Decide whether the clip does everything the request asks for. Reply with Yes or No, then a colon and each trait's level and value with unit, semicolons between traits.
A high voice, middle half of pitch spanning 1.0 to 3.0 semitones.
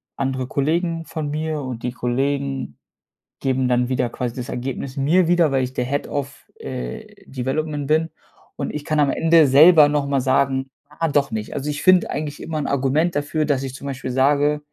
No: medium, 140 Hz; average, 2.7 semitones